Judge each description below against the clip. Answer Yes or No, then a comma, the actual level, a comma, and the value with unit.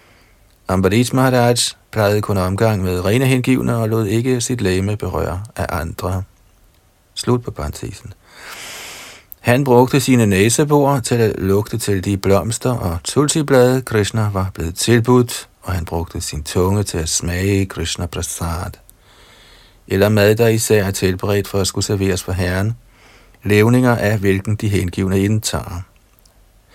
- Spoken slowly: Yes, slow, 140 wpm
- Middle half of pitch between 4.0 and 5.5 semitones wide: No, average, 3.5 semitones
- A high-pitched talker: No, low, 100 Hz